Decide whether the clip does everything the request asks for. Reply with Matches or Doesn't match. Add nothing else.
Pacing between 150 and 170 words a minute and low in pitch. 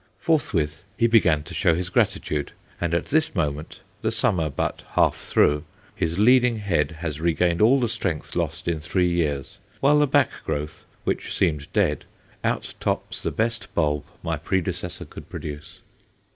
Matches